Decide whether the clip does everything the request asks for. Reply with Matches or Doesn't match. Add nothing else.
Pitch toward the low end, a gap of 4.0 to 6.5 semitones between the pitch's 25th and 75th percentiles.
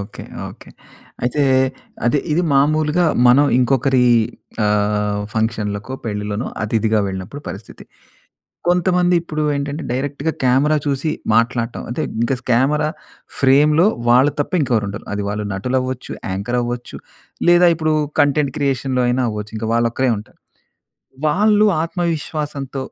Matches